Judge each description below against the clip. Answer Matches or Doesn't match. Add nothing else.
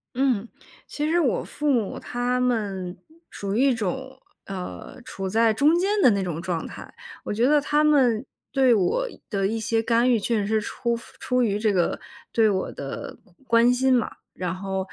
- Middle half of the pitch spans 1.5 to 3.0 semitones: Doesn't match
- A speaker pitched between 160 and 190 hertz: Doesn't match